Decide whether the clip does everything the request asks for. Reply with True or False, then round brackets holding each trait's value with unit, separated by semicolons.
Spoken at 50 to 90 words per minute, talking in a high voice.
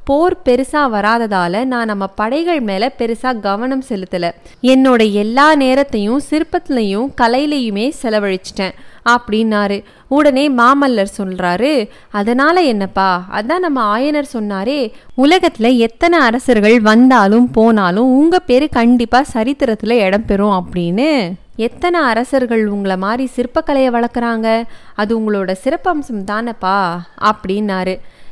False (105 wpm; 235 Hz)